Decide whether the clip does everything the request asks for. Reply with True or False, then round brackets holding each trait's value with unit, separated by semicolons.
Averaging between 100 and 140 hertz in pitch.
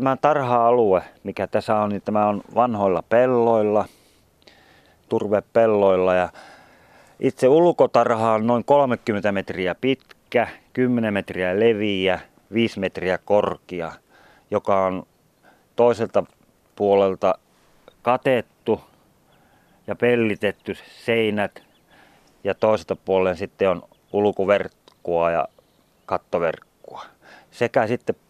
True (105 Hz)